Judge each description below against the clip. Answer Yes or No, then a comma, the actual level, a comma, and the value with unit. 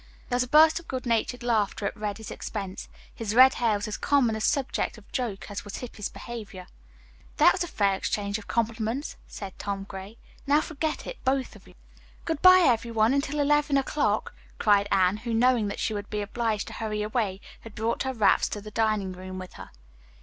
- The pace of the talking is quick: Yes, fast, 210 wpm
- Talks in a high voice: Yes, high, 225 Hz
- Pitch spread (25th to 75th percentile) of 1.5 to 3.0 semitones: No, average, 4.0 semitones